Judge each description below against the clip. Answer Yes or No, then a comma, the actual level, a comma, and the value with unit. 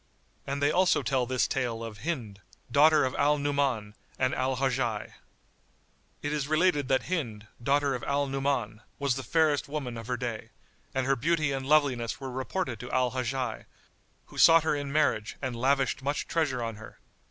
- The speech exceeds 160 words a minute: Yes, average, 180 wpm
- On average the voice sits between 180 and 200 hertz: No, low, 135 Hz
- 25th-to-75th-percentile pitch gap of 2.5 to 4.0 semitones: Yes, average, 2.9 semitones